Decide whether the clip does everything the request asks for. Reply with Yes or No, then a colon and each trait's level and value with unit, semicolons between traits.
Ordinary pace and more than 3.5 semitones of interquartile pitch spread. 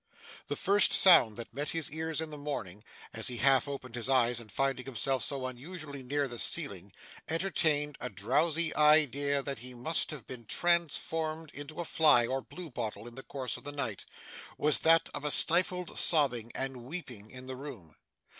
Yes: average, 185 wpm; average, 4.2 semitones